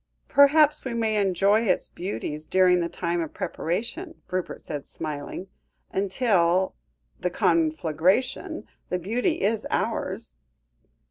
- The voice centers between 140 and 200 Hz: Yes, medium, 185 Hz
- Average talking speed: No, slow, 120 wpm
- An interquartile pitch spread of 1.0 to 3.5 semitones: No, average, 5.1 semitones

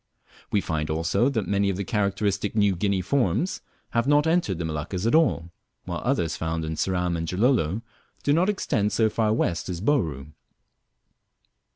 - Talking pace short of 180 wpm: Yes, average, 165 wpm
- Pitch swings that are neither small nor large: No, wide, 5.8 semitones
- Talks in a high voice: No, low, 100 Hz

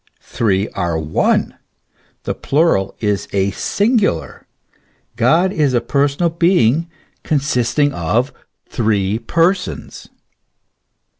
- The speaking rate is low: Yes, slow, 95 wpm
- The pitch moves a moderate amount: No, wide, 8.5 semitones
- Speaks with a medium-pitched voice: No, low, 125 Hz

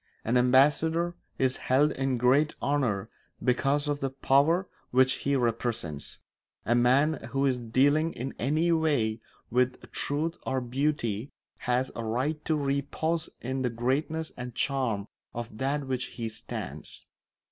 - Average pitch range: Yes, average, 3.3 semitones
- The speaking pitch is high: No, low, 130 Hz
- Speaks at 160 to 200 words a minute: No, average, 145 wpm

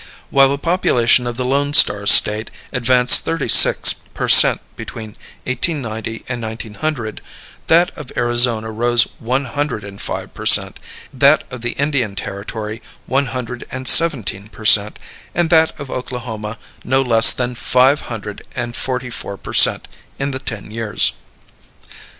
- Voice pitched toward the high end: No, low, 120 Hz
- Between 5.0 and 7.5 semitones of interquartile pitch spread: No, average, 3.3 semitones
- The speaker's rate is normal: Yes, average, 150 wpm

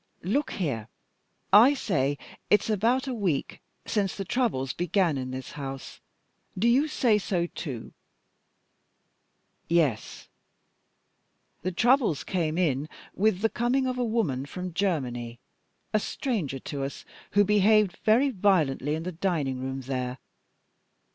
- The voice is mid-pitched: Yes, medium, 180 Hz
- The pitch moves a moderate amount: No, wide, 7.9 semitones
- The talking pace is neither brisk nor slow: No, slow, 130 wpm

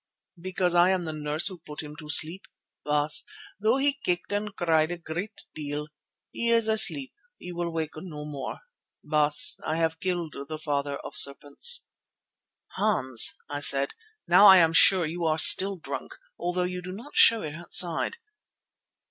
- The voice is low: No, medium, 170 Hz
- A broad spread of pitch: No, average, 3.8 semitones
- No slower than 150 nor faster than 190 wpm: Yes, average, 170 wpm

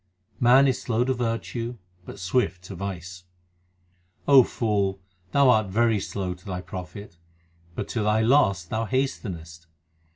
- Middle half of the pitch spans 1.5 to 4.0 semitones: No, average, 4.8 semitones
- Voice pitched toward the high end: No, low, 105 Hz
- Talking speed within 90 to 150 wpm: Yes, average, 140 wpm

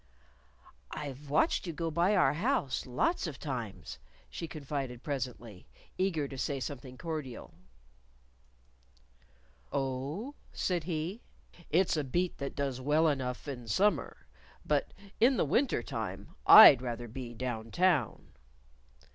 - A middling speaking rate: No, slow, 120 wpm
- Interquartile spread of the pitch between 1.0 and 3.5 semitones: No, average, 4.9 semitones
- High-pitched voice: No, medium, 140 Hz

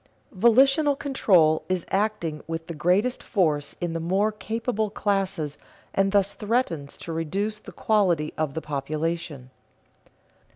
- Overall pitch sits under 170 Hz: No, medium, 185 Hz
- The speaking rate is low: Yes, slow, 130 wpm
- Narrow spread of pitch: No, average, 5.0 semitones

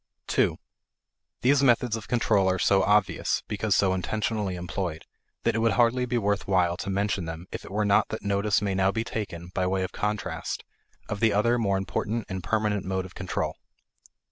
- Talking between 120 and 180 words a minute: No, average, 195 wpm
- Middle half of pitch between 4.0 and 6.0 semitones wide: No, narrow, 2.6 semitones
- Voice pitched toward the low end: Yes, low, 100 Hz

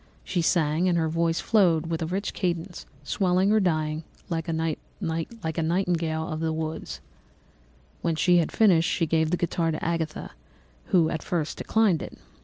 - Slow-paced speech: No, average, 170 wpm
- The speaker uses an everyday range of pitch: No, narrow, 1.9 semitones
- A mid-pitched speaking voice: Yes, medium, 165 Hz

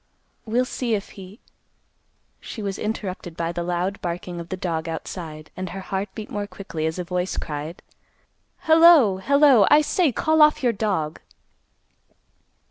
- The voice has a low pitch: No, high, 190 Hz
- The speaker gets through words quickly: No, average, 155 wpm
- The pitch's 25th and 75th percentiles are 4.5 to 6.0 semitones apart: Yes, average, 5.1 semitones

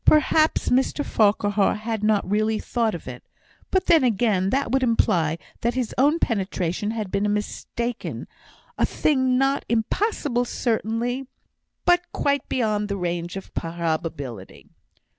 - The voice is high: Yes, high, 220 Hz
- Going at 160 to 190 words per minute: No, slow, 135 wpm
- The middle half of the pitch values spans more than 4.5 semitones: Yes, average, 4.9 semitones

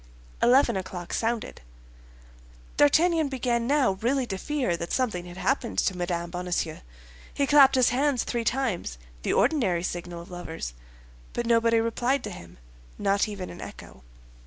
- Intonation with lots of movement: Yes, wide, 6.7 semitones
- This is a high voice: Yes, high, 230 Hz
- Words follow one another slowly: No, average, 145 wpm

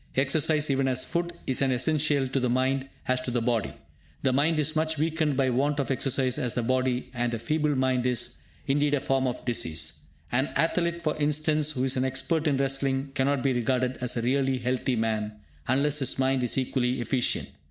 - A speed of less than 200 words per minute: No, fast, 205 wpm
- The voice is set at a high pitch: No, low, 135 Hz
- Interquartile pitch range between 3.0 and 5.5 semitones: No, narrow, 2.5 semitones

